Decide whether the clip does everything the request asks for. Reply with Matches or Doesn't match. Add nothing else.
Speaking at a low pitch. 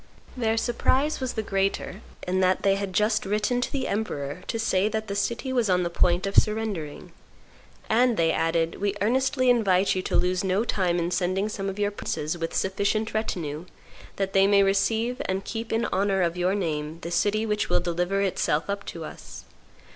Doesn't match